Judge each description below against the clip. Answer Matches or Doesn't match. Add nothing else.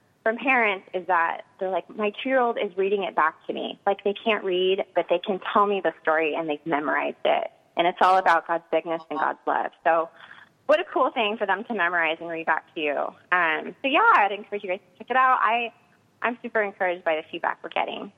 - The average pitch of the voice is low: Doesn't match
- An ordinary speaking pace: Doesn't match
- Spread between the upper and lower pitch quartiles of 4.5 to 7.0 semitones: Matches